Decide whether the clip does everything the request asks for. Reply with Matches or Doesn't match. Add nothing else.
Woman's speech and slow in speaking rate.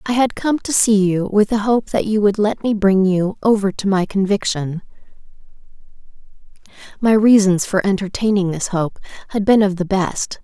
Doesn't match